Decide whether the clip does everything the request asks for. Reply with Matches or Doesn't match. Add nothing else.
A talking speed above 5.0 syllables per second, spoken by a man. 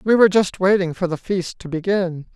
Matches